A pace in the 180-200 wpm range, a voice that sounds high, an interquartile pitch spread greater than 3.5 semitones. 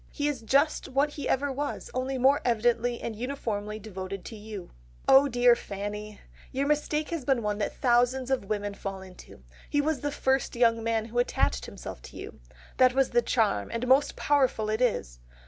Yes: average, 190 wpm; high, 240 Hz; average, 4.1 semitones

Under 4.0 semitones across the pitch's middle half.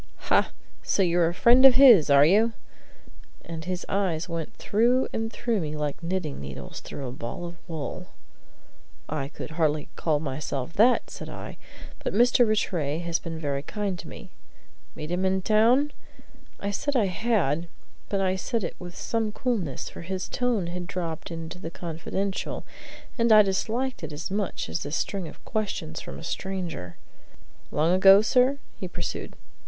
No: average, 5.2 semitones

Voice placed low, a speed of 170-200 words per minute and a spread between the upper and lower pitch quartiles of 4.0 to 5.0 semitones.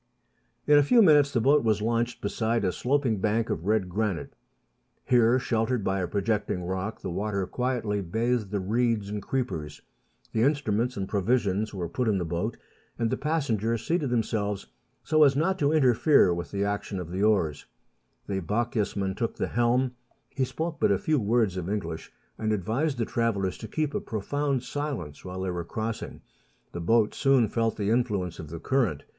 Yes: low, 110 Hz; average, 185 wpm; average, 4.4 semitones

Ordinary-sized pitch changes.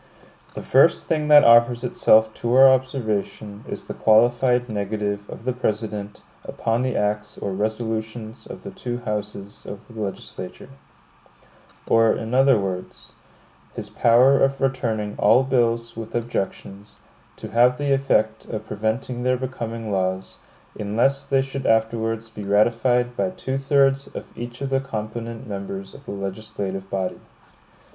Yes: average, 3.5 semitones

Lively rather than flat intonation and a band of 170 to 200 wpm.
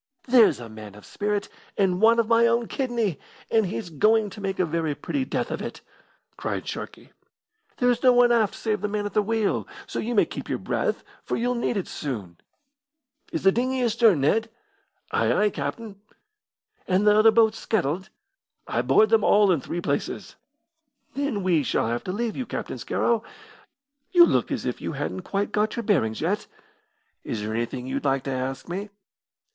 Yes: wide, 5.8 semitones; average, 190 wpm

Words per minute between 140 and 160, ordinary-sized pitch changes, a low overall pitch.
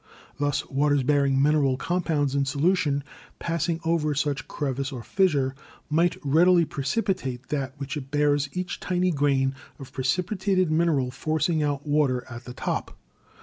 No: average, 145 wpm; average, 3.5 semitones; medium, 145 Hz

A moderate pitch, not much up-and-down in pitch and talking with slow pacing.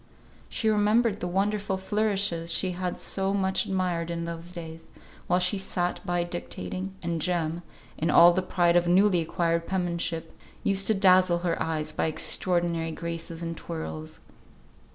No: medium, 175 Hz; narrow, 2.3 semitones; average, 155 wpm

